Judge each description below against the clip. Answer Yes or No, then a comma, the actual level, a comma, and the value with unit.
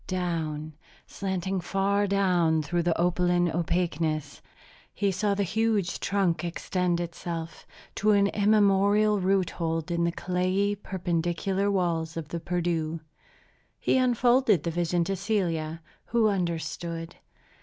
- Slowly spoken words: Yes, slow, 125 wpm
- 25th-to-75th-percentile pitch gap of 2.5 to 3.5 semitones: Yes, average, 3.0 semitones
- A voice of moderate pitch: Yes, medium, 180 Hz